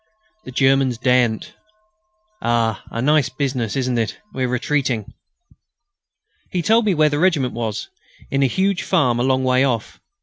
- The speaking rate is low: No, average, 155 wpm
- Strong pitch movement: No, average, 3.5 semitones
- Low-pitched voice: Yes, low, 130 Hz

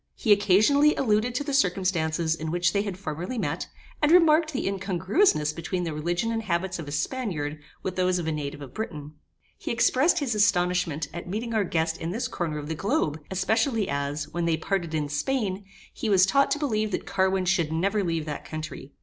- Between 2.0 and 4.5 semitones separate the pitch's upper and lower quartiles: No, wide, 5.5 semitones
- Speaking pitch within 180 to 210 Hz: Yes, medium, 185 Hz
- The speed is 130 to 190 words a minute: No, average, 200 wpm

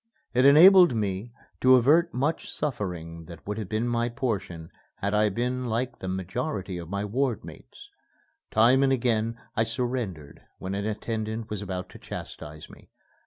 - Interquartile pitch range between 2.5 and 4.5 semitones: No, average, 4.9 semitones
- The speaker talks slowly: No, average, 165 wpm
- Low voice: Yes, low, 110 Hz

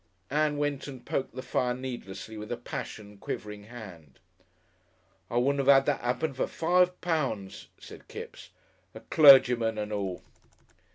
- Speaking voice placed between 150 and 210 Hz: No, low, 125 Hz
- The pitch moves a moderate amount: Yes, average, 4.9 semitones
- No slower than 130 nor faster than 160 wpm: Yes, average, 150 wpm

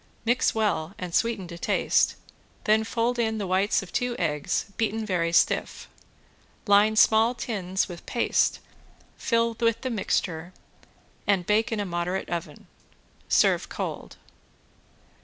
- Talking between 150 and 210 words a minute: No, slow, 135 wpm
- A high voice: Yes, high, 205 Hz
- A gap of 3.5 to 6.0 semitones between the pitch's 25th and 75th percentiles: Yes, average, 4.2 semitones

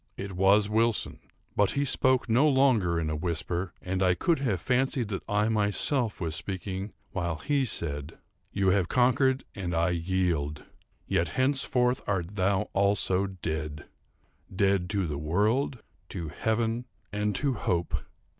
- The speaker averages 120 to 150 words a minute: Yes, average, 145 wpm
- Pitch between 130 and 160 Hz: No, low, 100 Hz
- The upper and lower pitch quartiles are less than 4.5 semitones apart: No, average, 5.0 semitones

